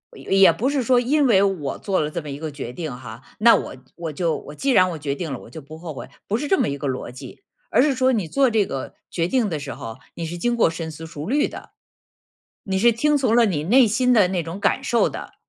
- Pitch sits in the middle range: Yes, medium, 180 Hz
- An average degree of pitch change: No, wide, 7.9 semitones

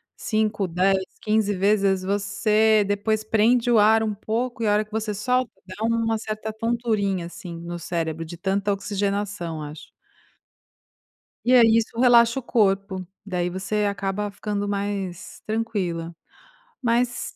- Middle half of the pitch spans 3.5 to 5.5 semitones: No, narrow, 2.5 semitones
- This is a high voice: Yes, high, 205 Hz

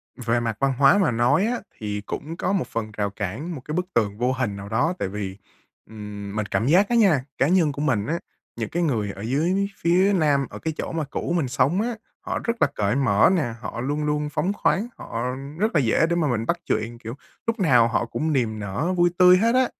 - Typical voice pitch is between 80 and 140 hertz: Yes, low, 135 Hz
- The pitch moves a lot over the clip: Yes, wide, 7.5 semitones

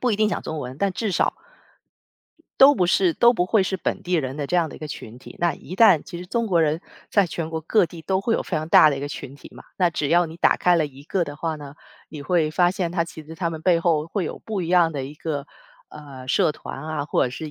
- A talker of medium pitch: Yes, medium, 165 Hz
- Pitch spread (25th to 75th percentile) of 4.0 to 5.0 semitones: No, average, 3.3 semitones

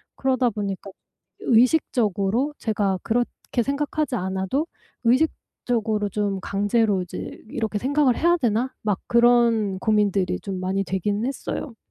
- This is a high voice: Yes, high, 220 Hz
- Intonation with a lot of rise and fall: No, average, 3.9 semitones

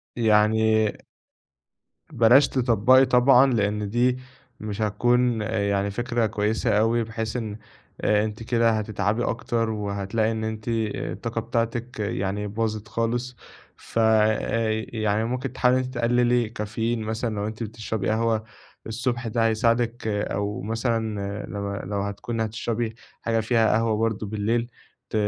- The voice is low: Yes, low, 110 Hz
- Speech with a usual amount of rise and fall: No, narrow, 1.8 semitones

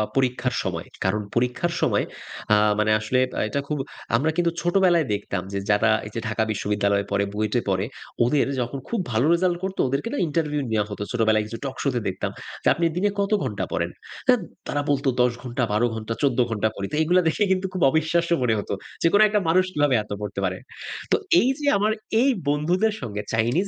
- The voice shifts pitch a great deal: Yes, wide, 8.0 semitones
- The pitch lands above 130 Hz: No, low, 125 Hz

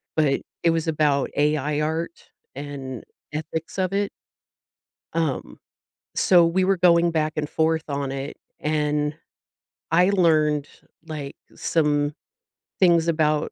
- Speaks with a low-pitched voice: No, medium, 155 Hz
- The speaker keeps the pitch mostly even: Yes, narrow, 2.2 semitones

